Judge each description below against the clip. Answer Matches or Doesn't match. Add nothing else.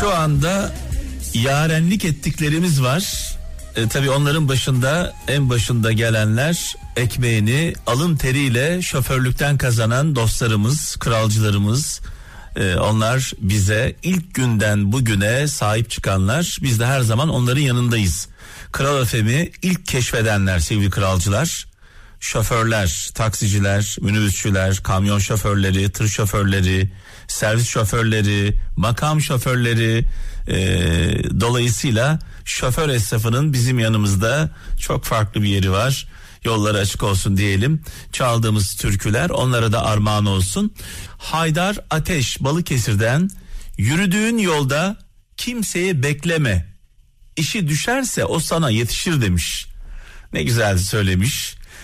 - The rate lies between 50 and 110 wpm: Matches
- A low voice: Matches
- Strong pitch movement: Matches